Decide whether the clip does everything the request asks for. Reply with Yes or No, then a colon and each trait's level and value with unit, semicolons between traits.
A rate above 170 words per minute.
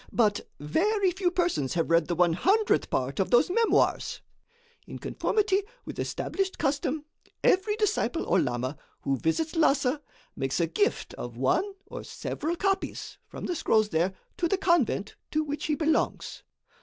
No: average, 155 wpm